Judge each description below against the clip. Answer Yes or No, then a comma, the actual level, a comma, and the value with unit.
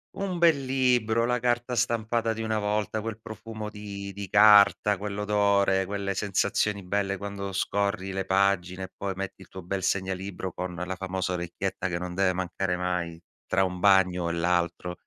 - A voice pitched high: No, low, 100 Hz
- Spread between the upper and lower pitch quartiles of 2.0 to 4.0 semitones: Yes, narrow, 2.4 semitones